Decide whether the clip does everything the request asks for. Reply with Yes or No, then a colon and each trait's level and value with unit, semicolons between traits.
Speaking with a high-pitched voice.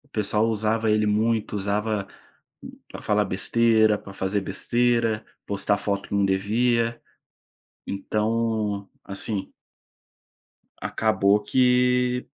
No: low, 110 Hz